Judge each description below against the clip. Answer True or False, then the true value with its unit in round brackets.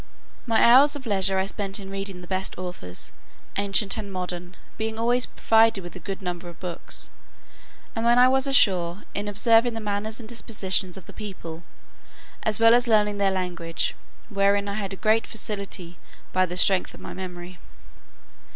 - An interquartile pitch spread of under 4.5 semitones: True (3.3 semitones)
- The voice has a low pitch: False (200 Hz)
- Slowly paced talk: False (180 wpm)